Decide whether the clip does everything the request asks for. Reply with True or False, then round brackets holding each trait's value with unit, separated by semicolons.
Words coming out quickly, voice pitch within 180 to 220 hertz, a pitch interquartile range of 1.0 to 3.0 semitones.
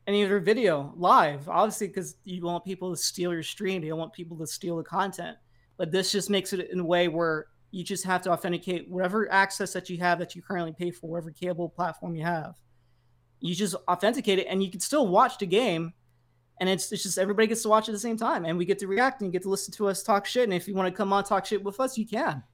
True (270 wpm; 185 Hz; 2.7 semitones)